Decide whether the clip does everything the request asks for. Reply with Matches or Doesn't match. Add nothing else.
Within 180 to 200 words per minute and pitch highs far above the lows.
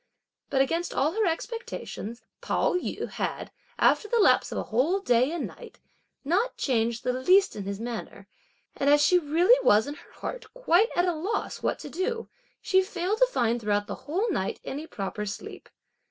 Matches